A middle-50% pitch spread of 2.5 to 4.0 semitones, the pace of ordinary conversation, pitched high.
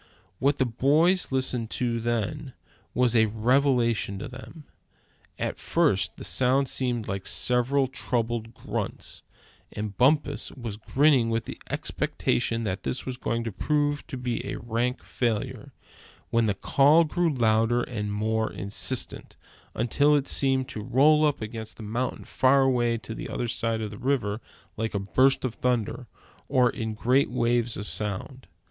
No: average, 3.2 semitones; average, 155 wpm; low, 120 Hz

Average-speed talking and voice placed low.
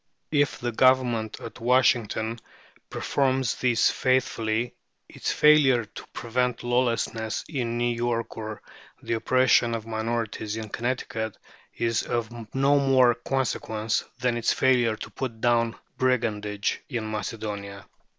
No: slow, 120 wpm; low, 120 Hz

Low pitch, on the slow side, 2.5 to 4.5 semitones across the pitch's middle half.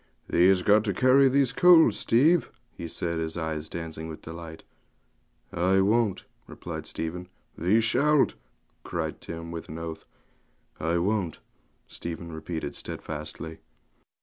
No: very low, 85 Hz; slow, 130 wpm; average, 5.1 semitones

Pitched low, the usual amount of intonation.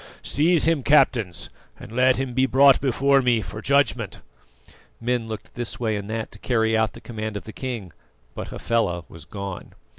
Yes: low, 115 Hz; average, 3.4 semitones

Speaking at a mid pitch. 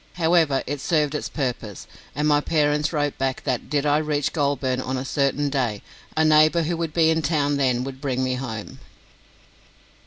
Yes: medium, 145 Hz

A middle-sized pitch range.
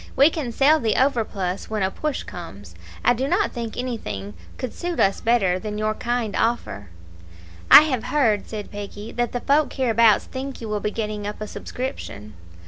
Yes: average, 3.9 semitones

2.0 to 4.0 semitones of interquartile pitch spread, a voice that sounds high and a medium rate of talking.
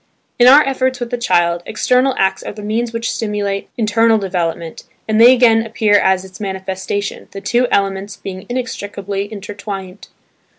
Yes: average, 3.2 semitones; high, 205 Hz; average, 160 wpm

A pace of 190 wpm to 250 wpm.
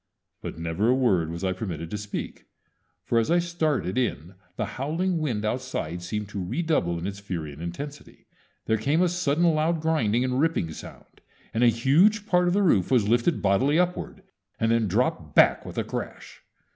Yes: average, 195 wpm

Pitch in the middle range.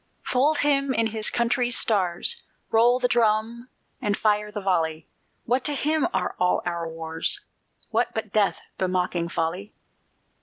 No: high, 215 Hz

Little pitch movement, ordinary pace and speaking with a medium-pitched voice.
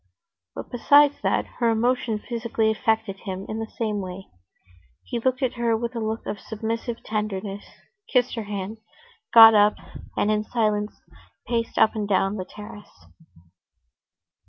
No: narrow, 2.0 semitones; average, 150 wpm; high, 220 Hz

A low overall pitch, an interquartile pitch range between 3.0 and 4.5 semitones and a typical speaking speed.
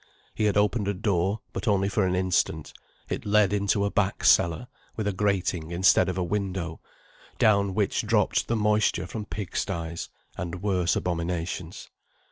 No: very low, 95 Hz; narrow, 2.6 semitones; average, 160 wpm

